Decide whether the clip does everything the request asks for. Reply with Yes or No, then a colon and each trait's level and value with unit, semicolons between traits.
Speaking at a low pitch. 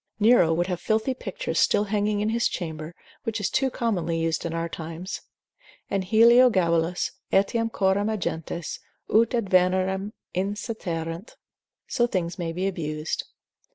No: high, 190 Hz